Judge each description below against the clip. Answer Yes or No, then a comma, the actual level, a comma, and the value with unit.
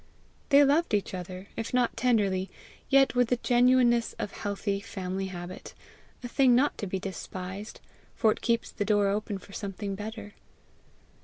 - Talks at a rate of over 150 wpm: Yes, average, 160 wpm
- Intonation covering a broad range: No, average, 3.9 semitones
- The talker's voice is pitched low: No, high, 210 Hz